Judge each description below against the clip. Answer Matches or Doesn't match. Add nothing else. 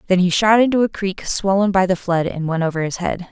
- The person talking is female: Matches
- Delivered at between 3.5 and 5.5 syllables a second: Doesn't match